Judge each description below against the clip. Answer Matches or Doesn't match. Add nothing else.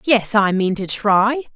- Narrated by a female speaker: Matches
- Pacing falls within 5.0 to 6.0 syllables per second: Doesn't match